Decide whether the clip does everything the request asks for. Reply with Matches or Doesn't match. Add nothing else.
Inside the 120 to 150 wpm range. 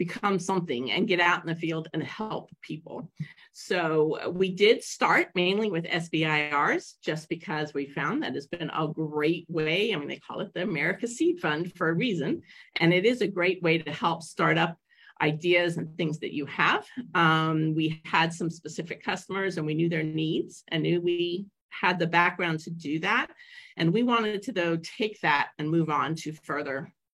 Doesn't match